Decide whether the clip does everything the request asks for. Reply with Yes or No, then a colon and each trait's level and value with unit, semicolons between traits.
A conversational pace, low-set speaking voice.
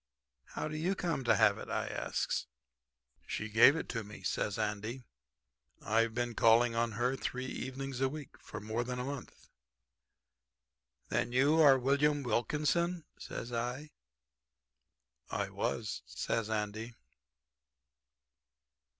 No: slow, 130 wpm; low, 120 Hz